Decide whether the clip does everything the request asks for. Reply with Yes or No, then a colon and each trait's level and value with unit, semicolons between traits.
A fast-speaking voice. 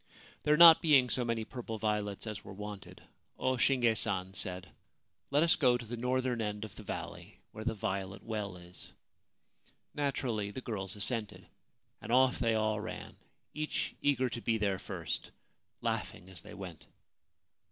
No: average, 165 wpm